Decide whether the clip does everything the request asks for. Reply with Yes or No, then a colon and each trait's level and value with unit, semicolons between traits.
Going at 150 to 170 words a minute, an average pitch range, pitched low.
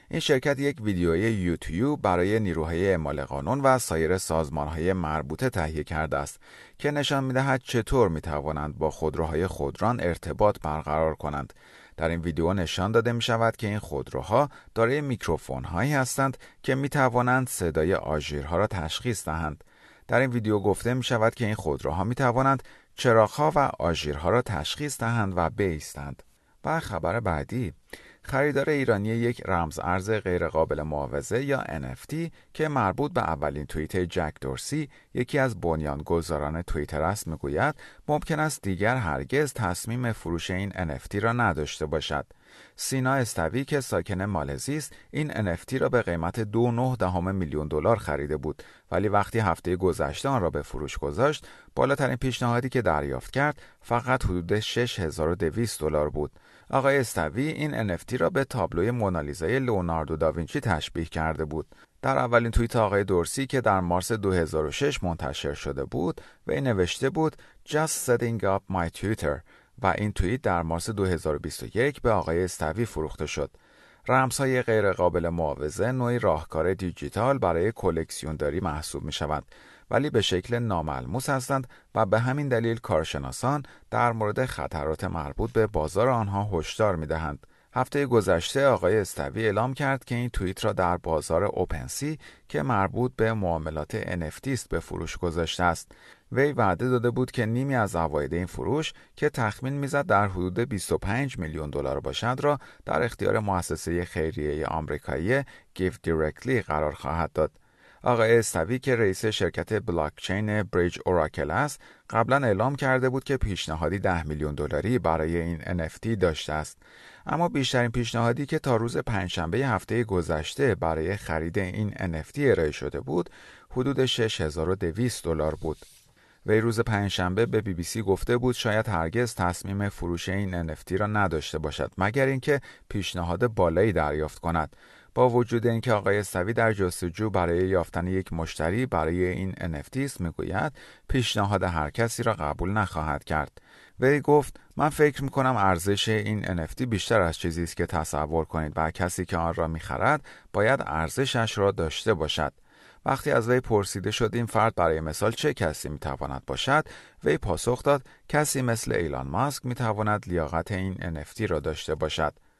No: fast, 155 wpm; wide, 6.9 semitones; very low, 95 Hz